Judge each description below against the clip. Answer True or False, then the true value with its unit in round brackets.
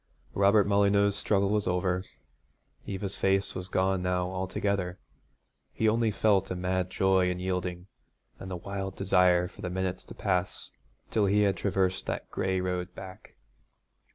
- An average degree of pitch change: False (1.5 semitones)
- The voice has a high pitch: False (95 Hz)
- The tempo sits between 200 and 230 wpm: False (155 wpm)